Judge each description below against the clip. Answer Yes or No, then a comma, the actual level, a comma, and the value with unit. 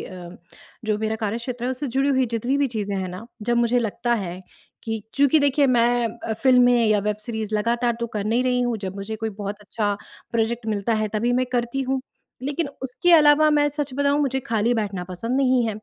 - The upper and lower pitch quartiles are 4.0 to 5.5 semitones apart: No, average, 3.3 semitones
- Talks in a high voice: Yes, high, 235 Hz